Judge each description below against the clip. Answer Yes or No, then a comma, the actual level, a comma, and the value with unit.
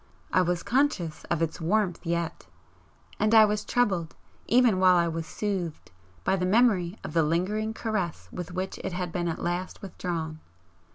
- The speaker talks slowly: No, average, 170 wpm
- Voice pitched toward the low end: No, medium, 180 Hz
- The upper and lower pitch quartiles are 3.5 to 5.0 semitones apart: Yes, average, 3.8 semitones